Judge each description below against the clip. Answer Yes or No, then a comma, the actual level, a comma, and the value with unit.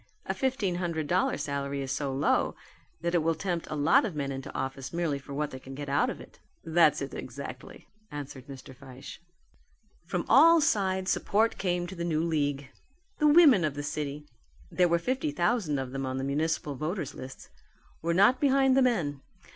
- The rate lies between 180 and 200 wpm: Yes, average, 195 wpm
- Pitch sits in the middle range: Yes, medium, 155 Hz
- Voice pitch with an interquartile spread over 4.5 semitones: Yes, average, 5.1 semitones